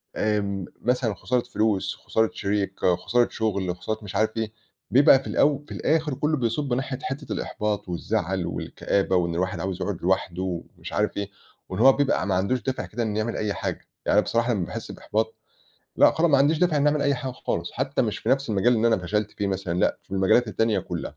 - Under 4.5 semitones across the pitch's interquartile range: No, average, 5.0 semitones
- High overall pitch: No, low, 110 Hz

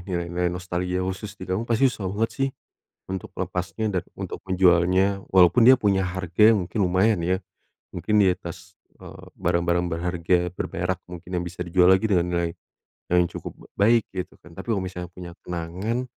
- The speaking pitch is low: Yes, very low, 90 Hz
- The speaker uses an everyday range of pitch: No, narrow, 1.9 semitones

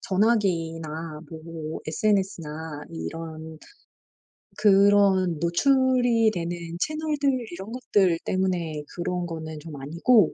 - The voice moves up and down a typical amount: Yes, average, 4.6 semitones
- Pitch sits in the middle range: Yes, medium, 175 Hz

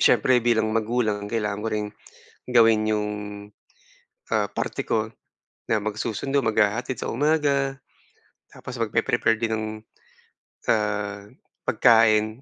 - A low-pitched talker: Yes, low, 110 Hz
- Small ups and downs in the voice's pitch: Yes, narrow, 2.2 semitones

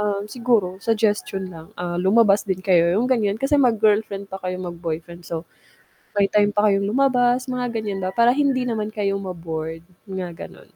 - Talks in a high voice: Yes, high, 200 Hz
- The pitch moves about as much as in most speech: Yes, average, 3.7 semitones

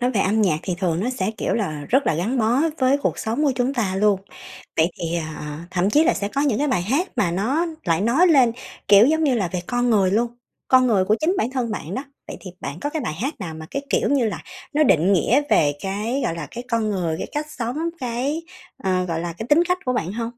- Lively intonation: Yes, wide, 6.1 semitones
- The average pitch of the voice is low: No, high, 225 Hz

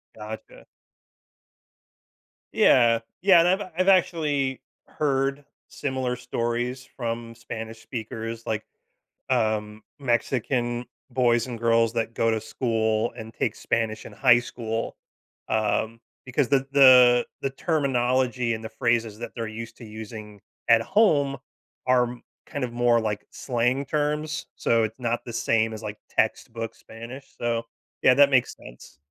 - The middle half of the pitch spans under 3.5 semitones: Yes, average, 2.7 semitones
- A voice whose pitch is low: Yes, low, 120 Hz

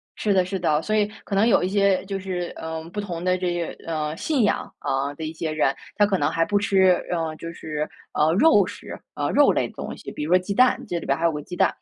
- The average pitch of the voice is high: No, medium, 180 Hz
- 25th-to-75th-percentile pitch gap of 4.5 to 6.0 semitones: No, average, 3.8 semitones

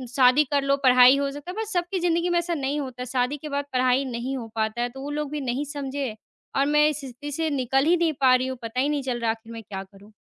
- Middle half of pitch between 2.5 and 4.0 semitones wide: Yes, average, 3.0 semitones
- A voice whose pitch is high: Yes, very high, 270 Hz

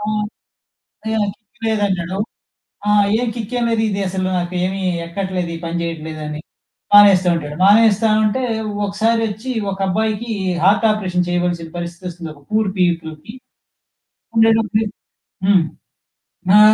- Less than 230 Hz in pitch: Yes, high, 195 Hz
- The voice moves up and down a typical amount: Yes, average, 3.8 semitones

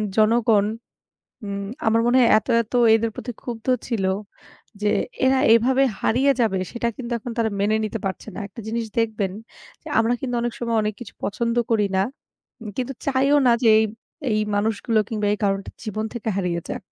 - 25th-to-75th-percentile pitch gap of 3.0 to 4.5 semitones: No, narrow, 2.4 semitones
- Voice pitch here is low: No, high, 225 Hz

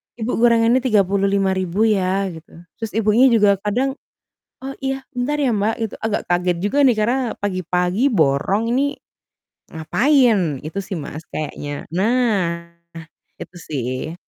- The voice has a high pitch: Yes, high, 205 Hz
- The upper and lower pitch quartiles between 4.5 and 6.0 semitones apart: Yes, average, 5.2 semitones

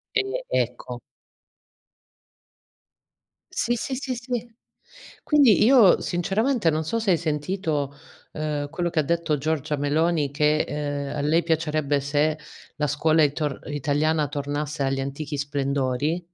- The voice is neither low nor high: Yes, medium, 155 Hz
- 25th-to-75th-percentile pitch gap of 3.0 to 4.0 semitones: Yes, average, 3.3 semitones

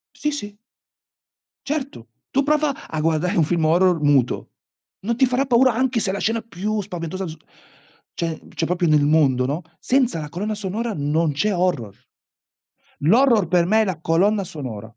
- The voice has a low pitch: No, medium, 180 Hz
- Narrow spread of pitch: No, wide, 6.3 semitones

